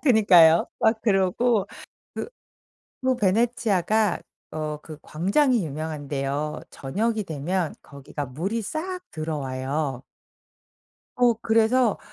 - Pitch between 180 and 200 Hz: Yes, medium, 185 Hz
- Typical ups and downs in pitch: No, wide, 6.9 semitones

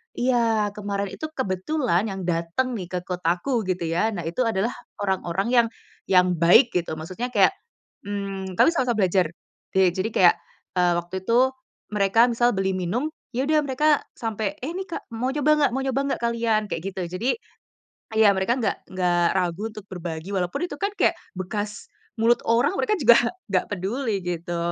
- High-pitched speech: Yes, high, 200 Hz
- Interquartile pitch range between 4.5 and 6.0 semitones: Yes, average, 4.9 semitones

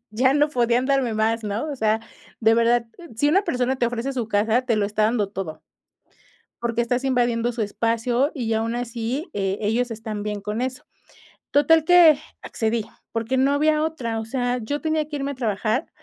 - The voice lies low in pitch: No, high, 240 Hz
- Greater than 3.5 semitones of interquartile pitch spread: No, average, 3.2 semitones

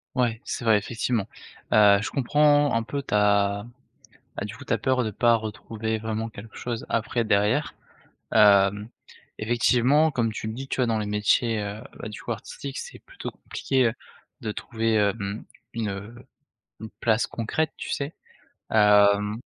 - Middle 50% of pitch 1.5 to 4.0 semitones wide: Yes, average, 2.8 semitones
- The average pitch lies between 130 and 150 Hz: No, low, 110 Hz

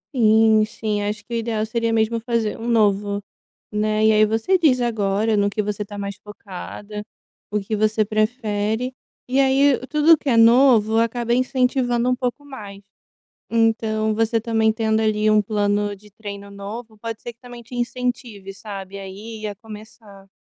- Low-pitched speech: No, high, 220 Hz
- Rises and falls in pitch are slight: Yes, narrow, 2.2 semitones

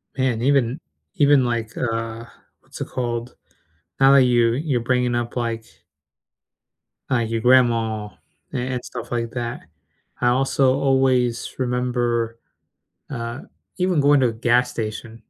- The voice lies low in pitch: Yes, low, 120 Hz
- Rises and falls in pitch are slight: Yes, narrow, 1.9 semitones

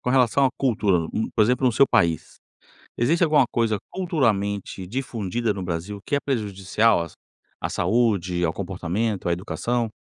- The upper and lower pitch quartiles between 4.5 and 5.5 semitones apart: Yes, average, 4.8 semitones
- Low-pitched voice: Yes, low, 110 Hz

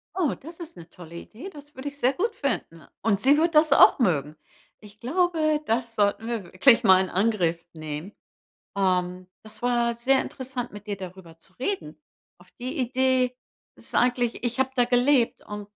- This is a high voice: Yes, high, 235 Hz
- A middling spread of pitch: No, wide, 5.9 semitones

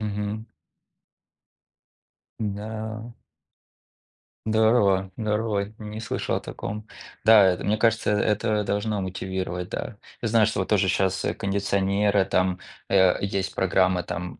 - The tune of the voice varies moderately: No, narrow, 2.3 semitones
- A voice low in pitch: Yes, low, 100 Hz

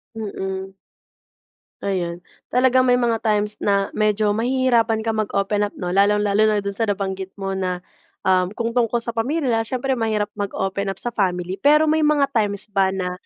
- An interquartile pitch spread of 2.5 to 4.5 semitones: Yes, average, 3.3 semitones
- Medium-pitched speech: No, high, 210 Hz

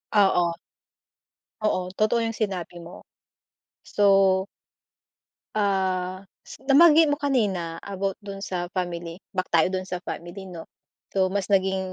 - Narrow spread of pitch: Yes, narrow, 2.1 semitones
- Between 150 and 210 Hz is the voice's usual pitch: Yes, high, 190 Hz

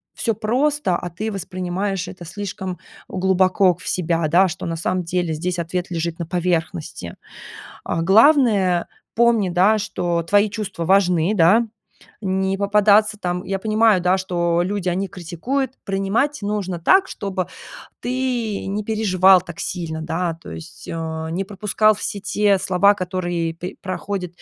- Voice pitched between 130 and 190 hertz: Yes, medium, 185 Hz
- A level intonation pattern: No, average, 3.0 semitones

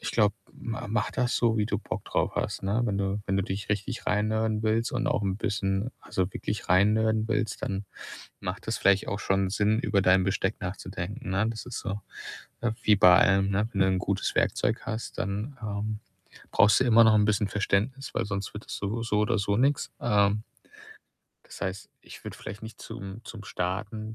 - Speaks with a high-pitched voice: No, low, 105 Hz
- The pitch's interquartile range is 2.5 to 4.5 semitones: No, narrow, 2.1 semitones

